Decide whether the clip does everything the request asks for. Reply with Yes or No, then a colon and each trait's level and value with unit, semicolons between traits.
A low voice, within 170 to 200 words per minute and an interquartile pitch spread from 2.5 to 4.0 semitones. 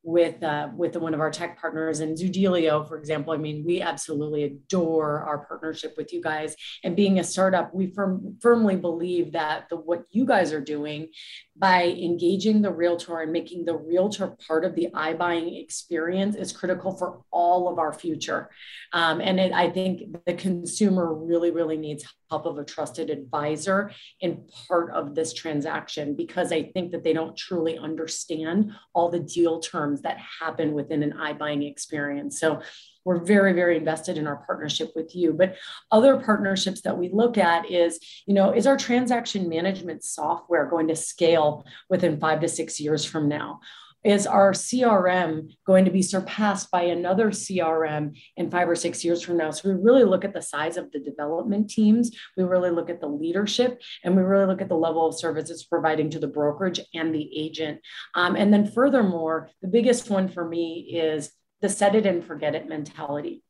No: medium, 170 Hz; average, 185 wpm; average, 3.1 semitones